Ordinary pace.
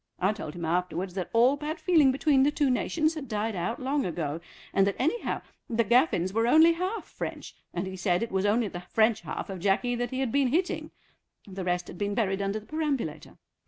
No: fast, 225 wpm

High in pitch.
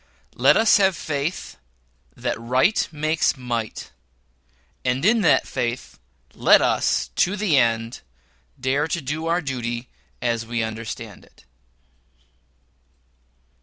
No: low, 130 Hz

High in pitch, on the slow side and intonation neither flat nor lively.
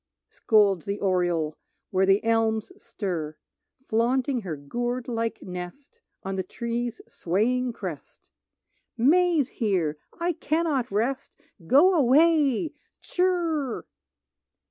No: high, 235 Hz; slow, 100 wpm; wide, 6.3 semitones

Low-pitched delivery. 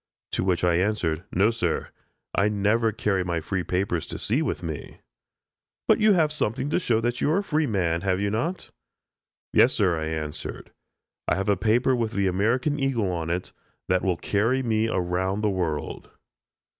Yes: low, 100 Hz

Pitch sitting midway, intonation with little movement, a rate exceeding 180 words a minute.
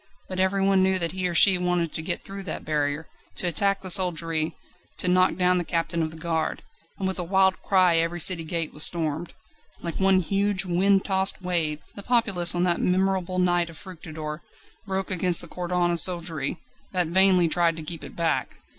Yes: medium, 180 Hz; narrow, 2.2 semitones; average, 200 wpm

